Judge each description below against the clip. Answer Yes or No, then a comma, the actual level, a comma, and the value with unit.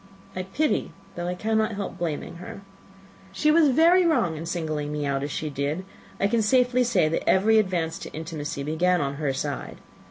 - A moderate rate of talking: Yes, average, 190 wpm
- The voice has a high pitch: No, medium, 180 Hz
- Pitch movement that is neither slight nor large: No, wide, 6.3 semitones